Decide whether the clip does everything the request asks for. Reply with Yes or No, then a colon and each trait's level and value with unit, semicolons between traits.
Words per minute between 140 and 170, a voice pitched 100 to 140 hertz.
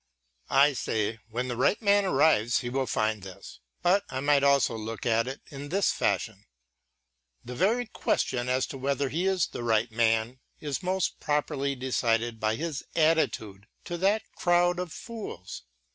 Yes: average, 165 wpm; low, 135 Hz